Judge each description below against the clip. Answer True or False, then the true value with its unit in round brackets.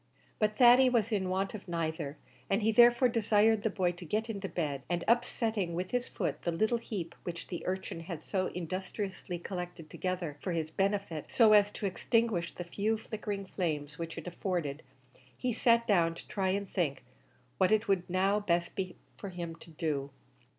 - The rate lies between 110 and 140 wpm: False (185 wpm)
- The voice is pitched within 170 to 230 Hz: True (190 Hz)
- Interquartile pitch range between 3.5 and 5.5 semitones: True (4.0 semitones)